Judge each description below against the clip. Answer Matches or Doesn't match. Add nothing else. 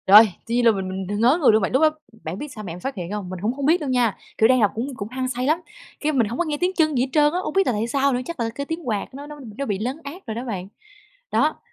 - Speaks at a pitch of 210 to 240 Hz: Doesn't match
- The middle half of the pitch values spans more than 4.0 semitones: Matches